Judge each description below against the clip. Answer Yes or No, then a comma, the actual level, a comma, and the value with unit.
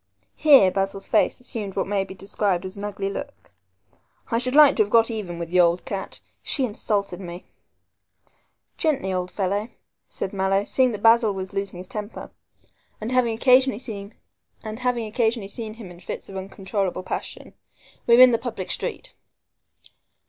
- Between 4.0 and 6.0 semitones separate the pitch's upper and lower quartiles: No, average, 3.5 semitones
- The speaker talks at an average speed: Yes, average, 155 wpm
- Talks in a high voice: Yes, high, 205 Hz